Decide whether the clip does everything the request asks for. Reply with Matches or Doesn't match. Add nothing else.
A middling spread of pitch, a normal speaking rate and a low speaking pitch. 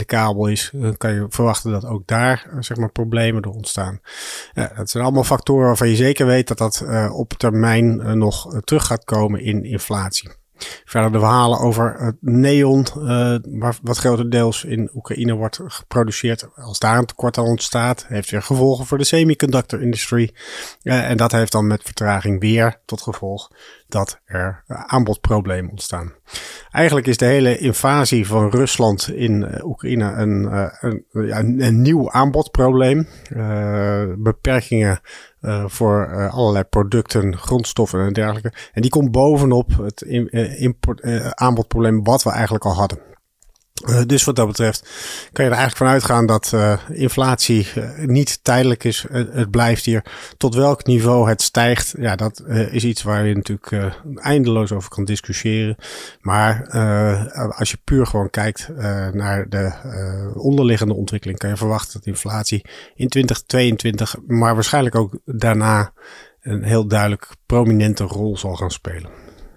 Matches